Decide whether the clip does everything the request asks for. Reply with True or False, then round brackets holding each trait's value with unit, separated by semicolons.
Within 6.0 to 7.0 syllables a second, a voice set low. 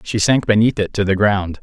False (5.2 syllables/s; 105 Hz)